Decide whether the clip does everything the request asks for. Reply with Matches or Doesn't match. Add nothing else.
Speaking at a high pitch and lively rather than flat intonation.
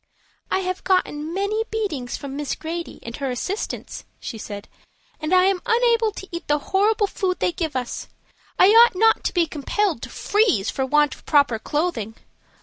Matches